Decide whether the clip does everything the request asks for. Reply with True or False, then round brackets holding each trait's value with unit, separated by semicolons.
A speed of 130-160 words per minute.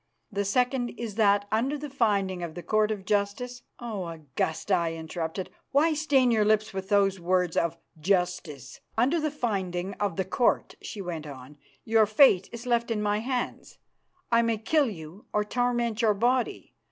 False (180 wpm)